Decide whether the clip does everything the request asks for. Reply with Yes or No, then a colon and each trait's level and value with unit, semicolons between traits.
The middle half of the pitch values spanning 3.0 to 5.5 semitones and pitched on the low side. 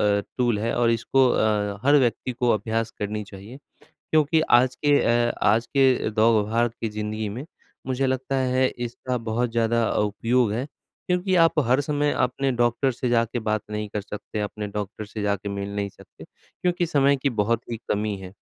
Yes: average, 3.5 semitones; low, 115 Hz